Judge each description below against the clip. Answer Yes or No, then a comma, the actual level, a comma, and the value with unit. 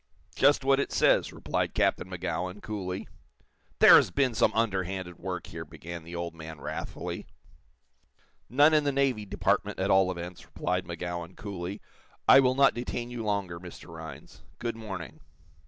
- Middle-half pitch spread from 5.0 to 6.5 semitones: Yes, average, 5.3 semitones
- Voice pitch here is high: No, very low, 95 Hz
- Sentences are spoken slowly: No, average, 155 wpm